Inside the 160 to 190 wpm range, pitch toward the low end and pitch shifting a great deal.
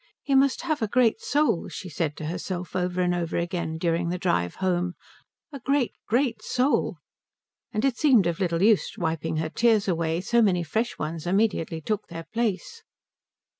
No: average, 175 wpm; medium, 185 Hz; wide, 5.9 semitones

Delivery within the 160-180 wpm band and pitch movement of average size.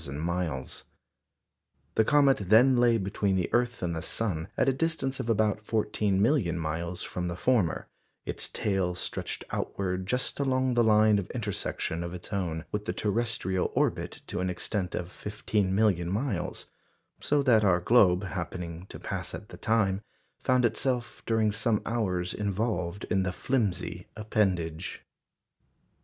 No: average, 150 wpm; average, 4.4 semitones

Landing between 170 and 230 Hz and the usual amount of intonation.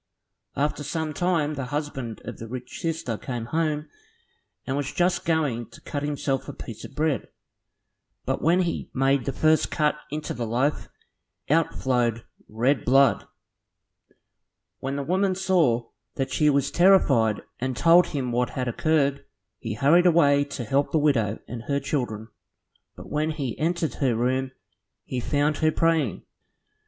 No: medium, 140 Hz; average, 4.0 semitones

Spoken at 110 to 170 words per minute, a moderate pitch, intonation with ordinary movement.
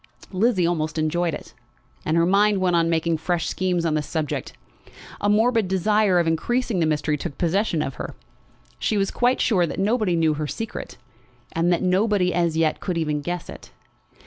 No: average, 185 wpm; medium, 175 Hz; average, 3.8 semitones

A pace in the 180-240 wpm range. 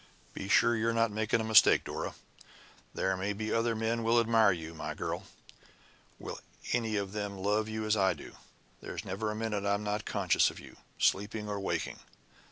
Yes: average, 185 wpm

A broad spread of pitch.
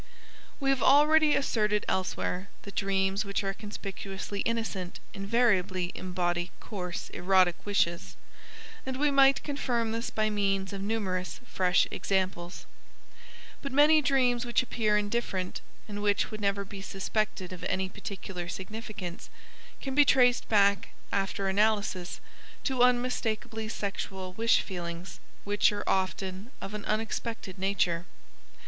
No: average, 3.5 semitones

